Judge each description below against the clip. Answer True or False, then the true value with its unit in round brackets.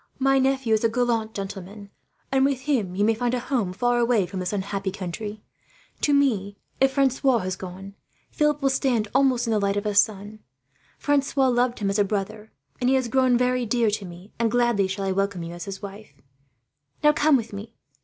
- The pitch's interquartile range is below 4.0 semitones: False (4.3 semitones)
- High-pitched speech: True (220 Hz)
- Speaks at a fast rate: True (210 wpm)